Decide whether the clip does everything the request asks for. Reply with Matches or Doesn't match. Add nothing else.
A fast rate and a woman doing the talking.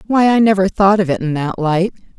Matches